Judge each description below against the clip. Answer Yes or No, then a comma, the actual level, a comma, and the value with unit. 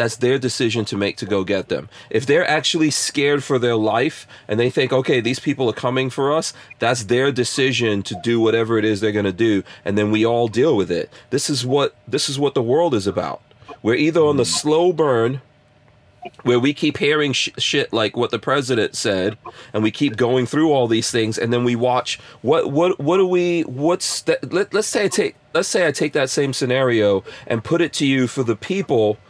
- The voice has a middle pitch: No, low, 125 Hz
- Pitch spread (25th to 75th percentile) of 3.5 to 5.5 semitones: Yes, average, 4.1 semitones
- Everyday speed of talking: No, fast, 225 wpm